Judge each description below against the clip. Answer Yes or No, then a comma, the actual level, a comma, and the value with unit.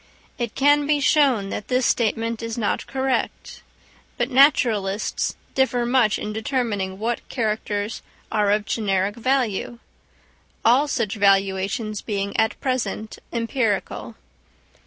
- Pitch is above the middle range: Yes, high, 225 Hz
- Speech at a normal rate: No, slow, 115 wpm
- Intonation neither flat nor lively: Yes, average, 3.7 semitones